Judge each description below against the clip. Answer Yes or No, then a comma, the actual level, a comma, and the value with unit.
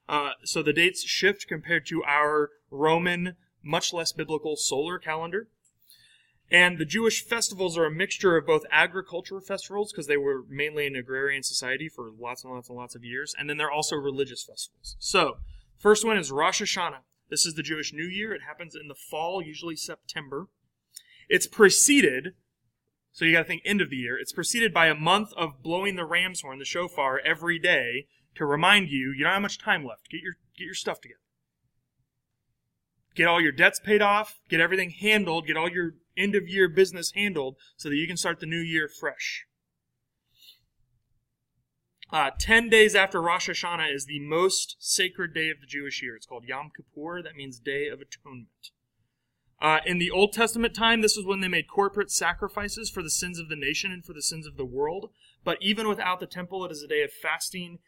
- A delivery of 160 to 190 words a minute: No, average, 200 wpm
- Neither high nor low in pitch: Yes, medium, 165 Hz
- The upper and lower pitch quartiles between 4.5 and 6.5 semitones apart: Yes, average, 5.0 semitones